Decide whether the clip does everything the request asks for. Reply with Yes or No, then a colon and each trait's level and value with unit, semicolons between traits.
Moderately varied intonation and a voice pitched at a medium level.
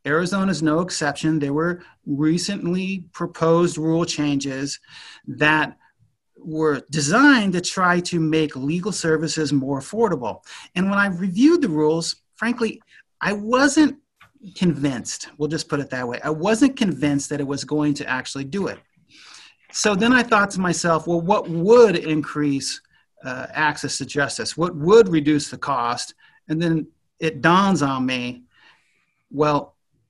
Yes: average, 4.7 semitones; medium, 160 Hz